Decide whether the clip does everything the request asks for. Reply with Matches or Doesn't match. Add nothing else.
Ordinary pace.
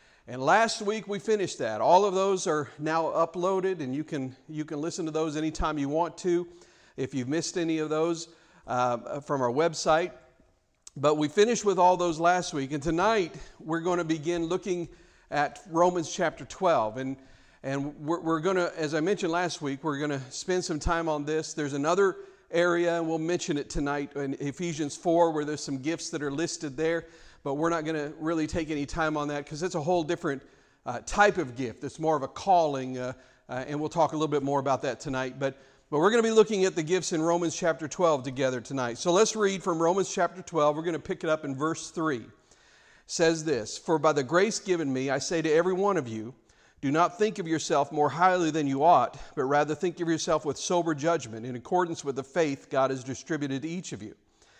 Doesn't match